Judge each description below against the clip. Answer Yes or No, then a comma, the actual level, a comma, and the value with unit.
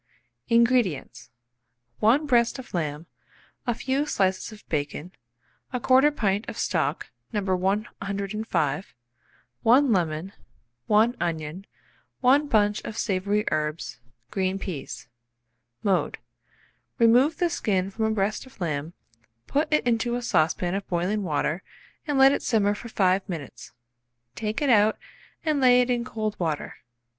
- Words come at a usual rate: No, slow, 130 wpm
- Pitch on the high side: Yes, high, 210 Hz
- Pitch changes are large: No, average, 4.9 semitones